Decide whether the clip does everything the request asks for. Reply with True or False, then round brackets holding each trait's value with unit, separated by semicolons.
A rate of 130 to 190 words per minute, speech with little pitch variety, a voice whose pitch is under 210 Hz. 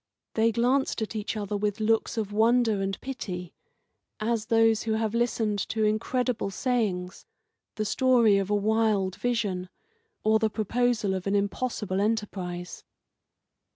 False (140 wpm; 2.3 semitones; 215 Hz)